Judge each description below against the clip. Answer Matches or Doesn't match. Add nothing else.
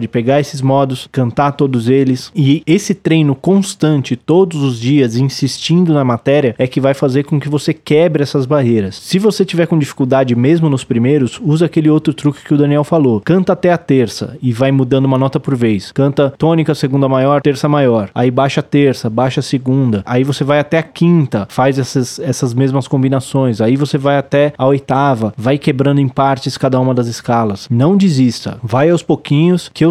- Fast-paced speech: Matches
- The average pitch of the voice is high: Doesn't match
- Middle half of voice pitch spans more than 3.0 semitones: Doesn't match